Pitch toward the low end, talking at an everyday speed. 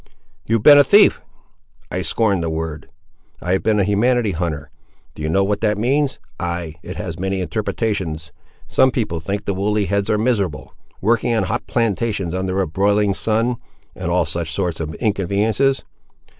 Yes: low, 100 Hz; average, 170 wpm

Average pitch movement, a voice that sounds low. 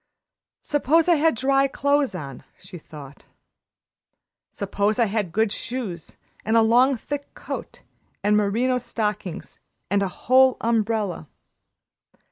No: average, 4.6 semitones; high, 225 Hz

